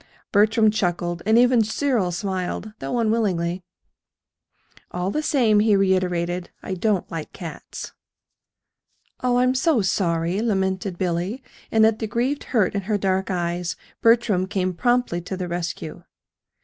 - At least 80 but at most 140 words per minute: Yes, slow, 135 wpm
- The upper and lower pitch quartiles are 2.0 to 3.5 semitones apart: No, average, 4.1 semitones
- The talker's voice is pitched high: Yes, high, 195 Hz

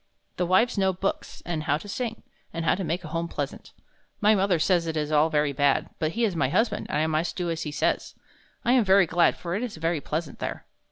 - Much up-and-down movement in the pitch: No, average, 3.8 semitones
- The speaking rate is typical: No, fast, 240 wpm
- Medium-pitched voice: Yes, medium, 170 Hz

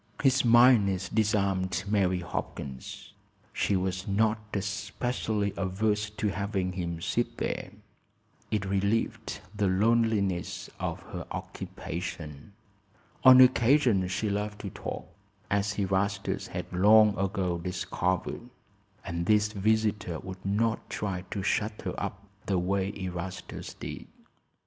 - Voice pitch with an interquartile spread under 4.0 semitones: Yes, narrow, 2.5 semitones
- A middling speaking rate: No, slow, 115 wpm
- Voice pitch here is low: Yes, low, 100 Hz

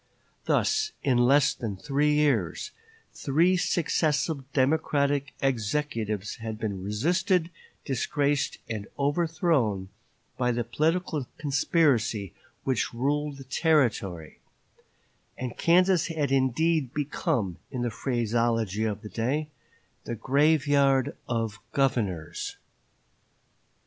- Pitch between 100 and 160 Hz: Yes, low, 135 Hz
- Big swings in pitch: No, average, 4.9 semitones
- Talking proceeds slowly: Yes, slow, 100 wpm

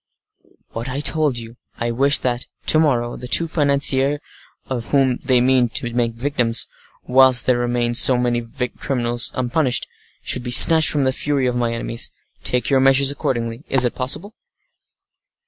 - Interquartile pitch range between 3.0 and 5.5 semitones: No, narrow, 2.4 semitones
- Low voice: Yes, low, 125 Hz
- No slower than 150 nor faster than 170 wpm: Yes, average, 160 wpm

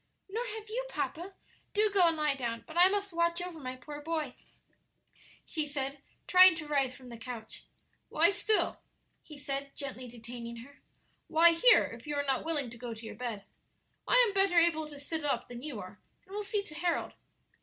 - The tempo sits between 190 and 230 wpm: Yes, average, 200 wpm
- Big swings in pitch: Yes, wide, 5.7 semitones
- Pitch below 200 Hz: No, very high, 300 Hz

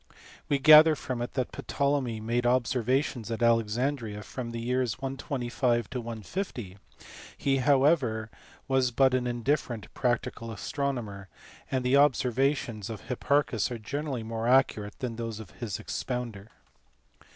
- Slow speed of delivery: Yes, slow, 130 wpm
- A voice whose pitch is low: Yes, low, 125 Hz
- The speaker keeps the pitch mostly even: No, average, 3.0 semitones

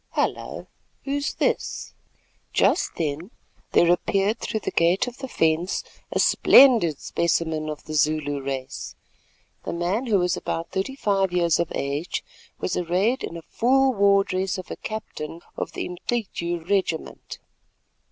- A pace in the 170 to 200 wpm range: No, average, 145 wpm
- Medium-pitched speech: Yes, medium, 180 Hz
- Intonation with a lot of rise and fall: No, average, 4.1 semitones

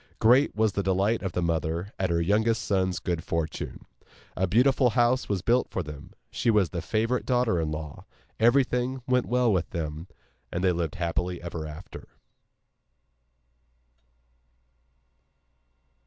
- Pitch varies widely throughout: Yes, wide, 5.8 semitones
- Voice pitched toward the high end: No, very low, 95 Hz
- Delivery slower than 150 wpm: Yes, average, 140 wpm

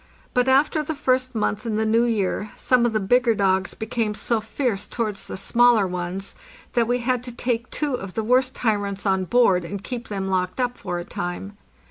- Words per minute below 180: No, fast, 205 wpm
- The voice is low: No, high, 225 Hz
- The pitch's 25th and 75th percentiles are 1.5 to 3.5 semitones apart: No, average, 4.1 semitones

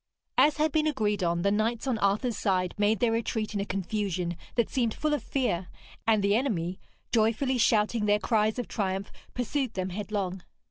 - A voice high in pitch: Yes, high, 215 Hz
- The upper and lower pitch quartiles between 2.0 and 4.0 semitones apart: Yes, average, 3.4 semitones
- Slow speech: No, average, 185 wpm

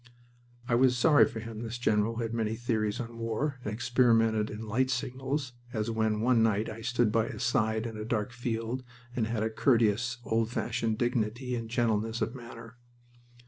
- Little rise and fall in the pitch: Yes, narrow, 1.8 semitones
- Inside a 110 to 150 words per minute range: No, average, 185 wpm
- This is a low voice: Yes, low, 115 Hz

